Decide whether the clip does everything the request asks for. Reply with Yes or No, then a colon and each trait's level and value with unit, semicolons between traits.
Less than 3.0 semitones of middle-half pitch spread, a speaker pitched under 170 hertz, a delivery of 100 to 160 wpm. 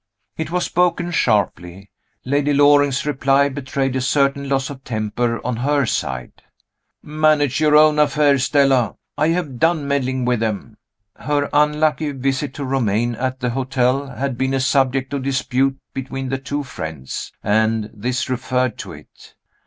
Yes: narrow, 2.6 semitones; low, 135 Hz; average, 155 wpm